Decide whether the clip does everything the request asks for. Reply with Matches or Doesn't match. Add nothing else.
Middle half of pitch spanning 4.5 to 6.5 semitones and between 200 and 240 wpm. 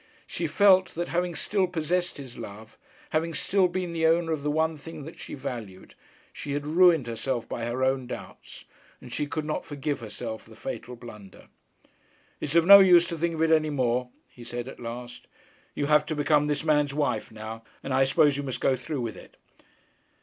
Matches